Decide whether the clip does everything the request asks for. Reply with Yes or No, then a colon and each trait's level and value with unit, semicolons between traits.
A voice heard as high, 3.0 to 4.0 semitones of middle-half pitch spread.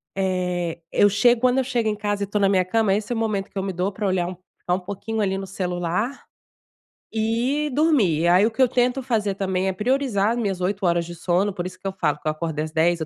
Yes: high, 195 Hz; average, 3.7 semitones